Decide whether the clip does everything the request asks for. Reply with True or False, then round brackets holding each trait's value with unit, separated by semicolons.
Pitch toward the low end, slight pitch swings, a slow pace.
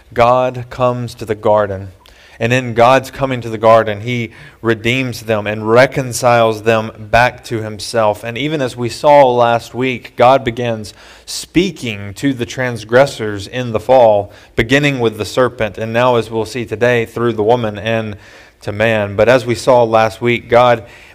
False (115 Hz; 2.1 semitones; 170 wpm)